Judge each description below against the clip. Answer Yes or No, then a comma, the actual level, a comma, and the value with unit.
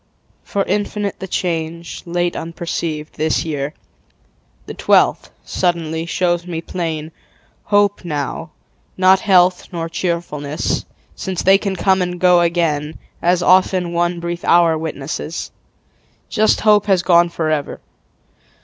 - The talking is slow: Yes, slow, 120 wpm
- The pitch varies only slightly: Yes, narrow, 2.3 semitones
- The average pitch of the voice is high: No, medium, 175 Hz